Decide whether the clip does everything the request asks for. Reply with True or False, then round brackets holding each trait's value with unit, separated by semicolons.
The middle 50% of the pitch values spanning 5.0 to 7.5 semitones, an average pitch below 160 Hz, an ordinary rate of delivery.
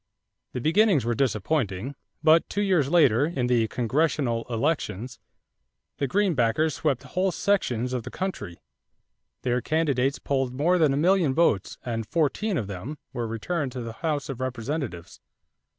True (5.4 semitones; 135 Hz; 150 wpm)